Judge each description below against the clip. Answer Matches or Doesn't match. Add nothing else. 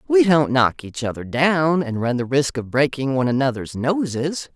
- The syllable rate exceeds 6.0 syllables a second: Doesn't match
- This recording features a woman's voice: Matches